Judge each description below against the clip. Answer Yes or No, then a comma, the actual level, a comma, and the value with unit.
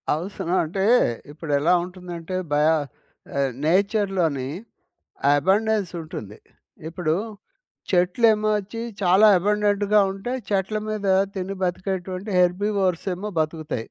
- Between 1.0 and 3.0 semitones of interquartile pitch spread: No, average, 3.6 semitones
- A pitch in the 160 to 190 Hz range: Yes, medium, 185 Hz